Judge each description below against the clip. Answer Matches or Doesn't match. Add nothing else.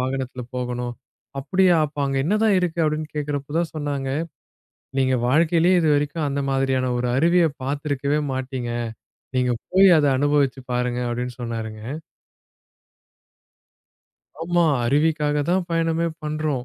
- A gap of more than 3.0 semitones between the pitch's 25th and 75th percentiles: Matches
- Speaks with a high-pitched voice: Doesn't match